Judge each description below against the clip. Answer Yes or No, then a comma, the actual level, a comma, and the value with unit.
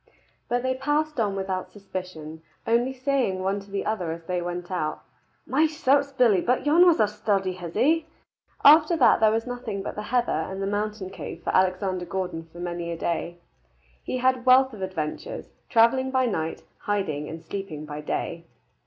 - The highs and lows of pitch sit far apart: Yes, wide, 6.4 semitones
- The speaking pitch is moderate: No, high, 200 Hz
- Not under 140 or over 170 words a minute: No, average, 180 wpm